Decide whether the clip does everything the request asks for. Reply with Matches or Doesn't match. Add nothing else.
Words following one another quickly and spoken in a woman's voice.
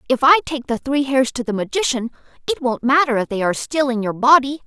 Matches